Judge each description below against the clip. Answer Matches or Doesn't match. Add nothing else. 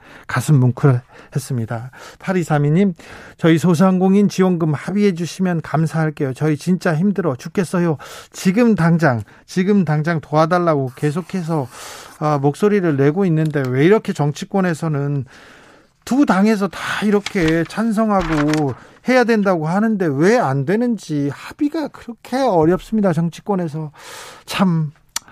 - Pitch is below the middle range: Doesn't match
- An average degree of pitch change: Matches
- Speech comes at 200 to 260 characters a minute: Doesn't match